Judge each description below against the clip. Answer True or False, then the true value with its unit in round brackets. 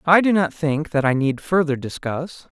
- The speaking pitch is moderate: True (155 Hz)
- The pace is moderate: False (210 wpm)